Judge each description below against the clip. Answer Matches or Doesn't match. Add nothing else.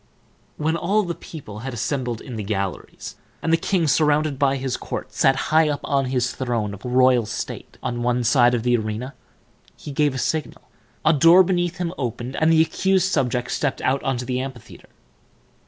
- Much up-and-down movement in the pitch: Doesn't match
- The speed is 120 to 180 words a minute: Doesn't match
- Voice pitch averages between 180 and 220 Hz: Doesn't match